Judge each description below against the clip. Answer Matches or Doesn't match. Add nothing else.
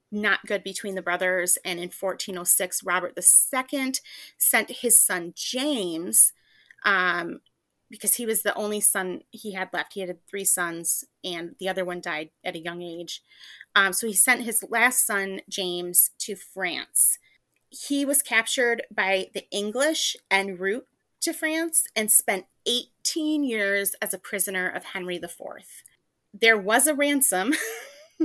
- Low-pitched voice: Doesn't match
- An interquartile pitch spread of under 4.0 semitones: Doesn't match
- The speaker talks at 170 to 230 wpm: Doesn't match